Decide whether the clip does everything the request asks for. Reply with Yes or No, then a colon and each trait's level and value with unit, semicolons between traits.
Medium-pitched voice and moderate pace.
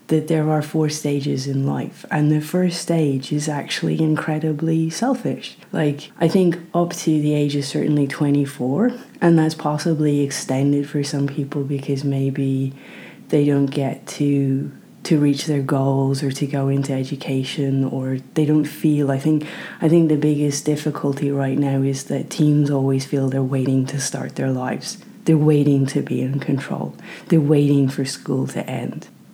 Yes: medium, 145 Hz; average, 170 wpm